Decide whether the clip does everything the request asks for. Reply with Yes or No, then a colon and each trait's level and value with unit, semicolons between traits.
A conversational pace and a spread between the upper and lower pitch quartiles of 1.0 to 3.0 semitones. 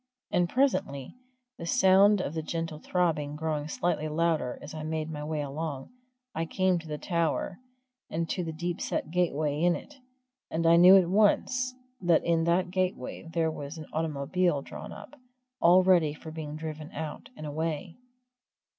Yes: average, 170 wpm; narrow, 2.6 semitones